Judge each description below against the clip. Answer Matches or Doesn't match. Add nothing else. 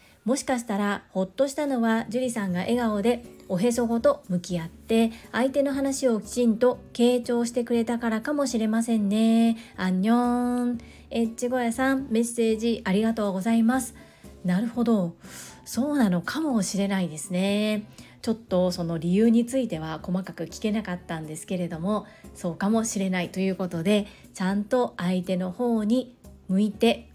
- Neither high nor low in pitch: Doesn't match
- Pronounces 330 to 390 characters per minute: Matches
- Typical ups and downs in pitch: Matches